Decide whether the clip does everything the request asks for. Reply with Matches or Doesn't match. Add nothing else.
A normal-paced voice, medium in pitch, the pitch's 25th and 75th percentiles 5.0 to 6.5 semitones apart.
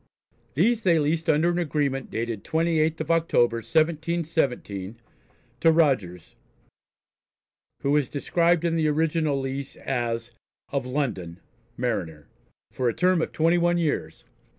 Doesn't match